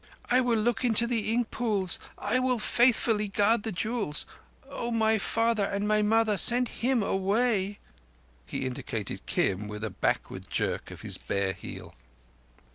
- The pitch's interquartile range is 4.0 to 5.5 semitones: No, average, 3.2 semitones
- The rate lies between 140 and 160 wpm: Yes, average, 150 wpm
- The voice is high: Yes, high, 220 Hz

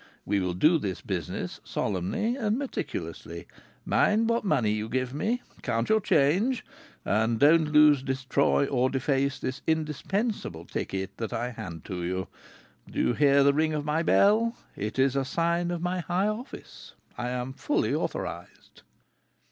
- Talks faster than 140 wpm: Yes, average, 155 wpm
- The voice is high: No, medium, 140 Hz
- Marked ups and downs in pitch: Yes, wide, 6.7 semitones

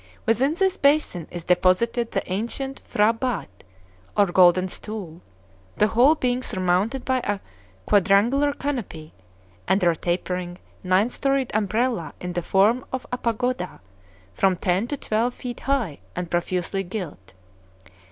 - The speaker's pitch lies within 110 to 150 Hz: No, high, 210 Hz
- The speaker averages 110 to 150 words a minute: Yes, slow, 135 wpm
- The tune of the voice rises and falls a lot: Yes, wide, 5.7 semitones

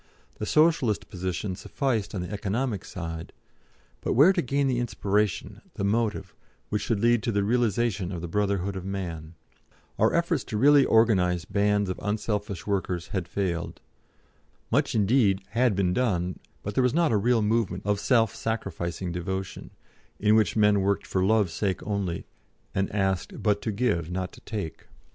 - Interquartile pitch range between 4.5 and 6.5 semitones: No, average, 3.4 semitones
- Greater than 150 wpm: Yes, average, 165 wpm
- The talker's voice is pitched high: No, low, 100 Hz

